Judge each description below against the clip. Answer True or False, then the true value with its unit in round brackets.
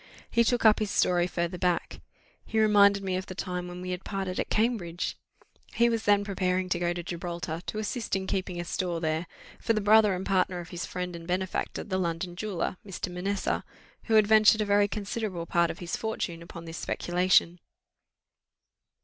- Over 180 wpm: True (195 wpm)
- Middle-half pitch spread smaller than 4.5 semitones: True (2.8 semitones)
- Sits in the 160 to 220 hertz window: True (185 Hz)